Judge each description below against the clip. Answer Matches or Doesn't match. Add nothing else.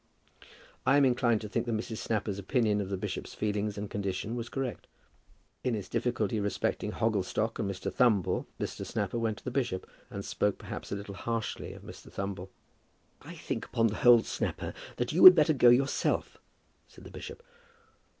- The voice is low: Matches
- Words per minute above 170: Matches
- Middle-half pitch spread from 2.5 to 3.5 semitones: Matches